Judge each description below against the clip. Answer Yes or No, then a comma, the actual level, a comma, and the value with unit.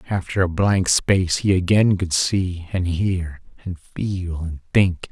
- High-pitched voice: No, very low, 90 Hz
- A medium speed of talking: Yes, average, 165 wpm